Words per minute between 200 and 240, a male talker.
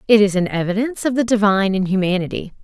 No: fast, 205 wpm; female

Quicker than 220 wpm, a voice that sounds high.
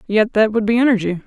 Yes: fast, 240 wpm; high, 215 Hz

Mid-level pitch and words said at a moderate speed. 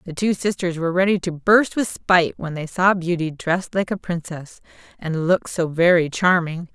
Yes: medium, 175 Hz; average, 195 wpm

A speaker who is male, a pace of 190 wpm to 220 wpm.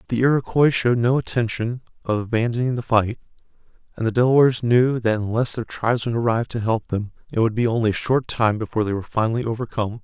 Yes: male; average, 195 wpm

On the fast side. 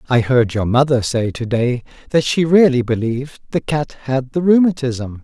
No: average, 185 wpm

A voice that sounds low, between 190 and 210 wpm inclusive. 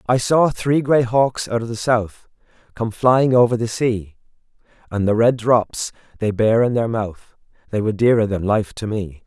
Yes: low, 115 Hz; average, 195 wpm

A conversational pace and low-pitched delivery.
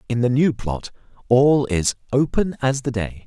Yes: average, 185 wpm; low, 125 Hz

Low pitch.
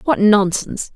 No: high, 210 Hz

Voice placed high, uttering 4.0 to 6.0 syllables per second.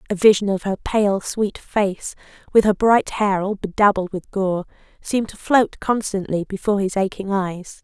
Yes: high, 200 Hz; 4.6 syllables/s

